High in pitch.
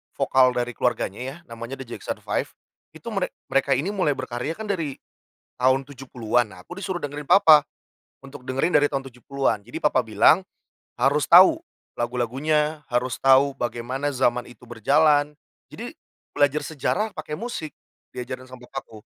No: low, 135 Hz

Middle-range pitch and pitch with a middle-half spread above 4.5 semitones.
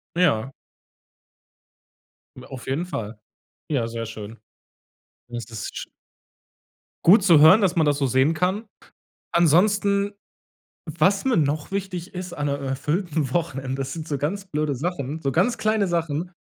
Yes: medium, 155 Hz; average, 5.2 semitones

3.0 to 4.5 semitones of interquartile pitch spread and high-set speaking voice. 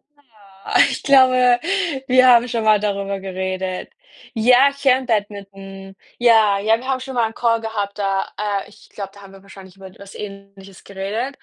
Yes: average, 3.8 semitones; high, 205 Hz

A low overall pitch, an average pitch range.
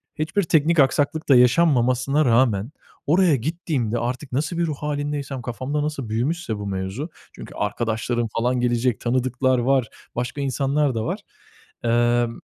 Yes: low, 130 Hz; average, 3.8 semitones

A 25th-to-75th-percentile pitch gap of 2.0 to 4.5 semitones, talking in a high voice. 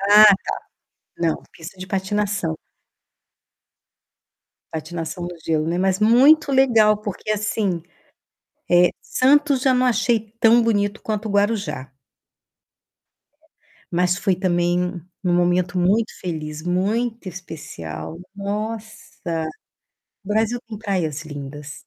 Yes: average, 4.0 semitones; high, 195 Hz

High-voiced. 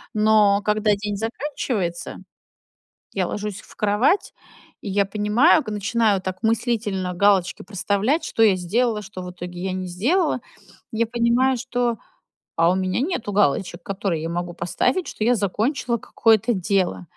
Yes: high, 210 Hz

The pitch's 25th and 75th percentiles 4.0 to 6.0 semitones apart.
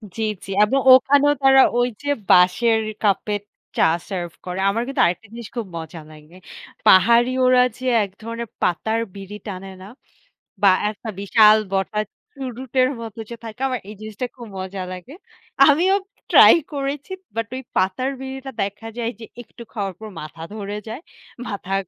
Yes: average, 4.7 semitones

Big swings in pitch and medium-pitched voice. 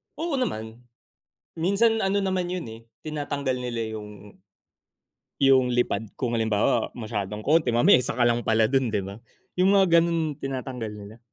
No: wide, 6.9 semitones; low, 125 Hz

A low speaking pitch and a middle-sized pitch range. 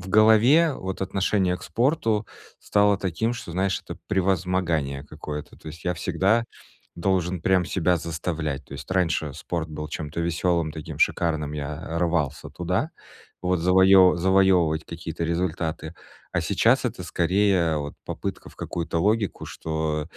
Yes: very low, 85 Hz; average, 3.2 semitones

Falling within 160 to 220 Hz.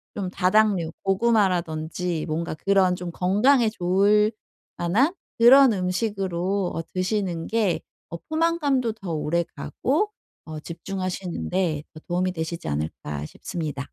Yes: medium, 185 Hz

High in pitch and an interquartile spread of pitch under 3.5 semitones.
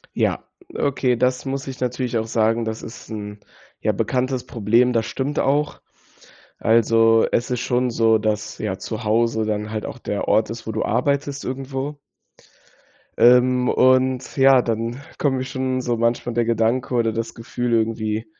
No: low, 120 Hz; narrow, 2.4 semitones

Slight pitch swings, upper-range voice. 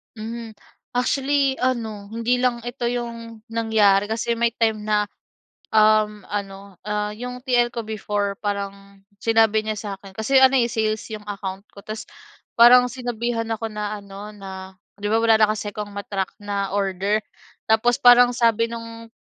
Yes: narrow, 2.3 semitones; high, 220 Hz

